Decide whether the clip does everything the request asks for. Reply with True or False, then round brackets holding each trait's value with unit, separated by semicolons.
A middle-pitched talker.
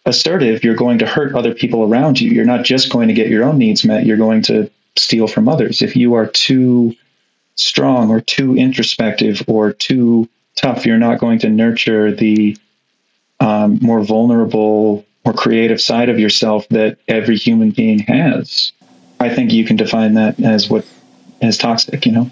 False (115 Hz)